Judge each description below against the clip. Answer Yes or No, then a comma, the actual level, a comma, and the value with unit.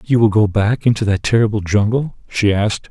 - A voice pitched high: No, low, 110 Hz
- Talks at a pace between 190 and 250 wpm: Yes, fast, 205 wpm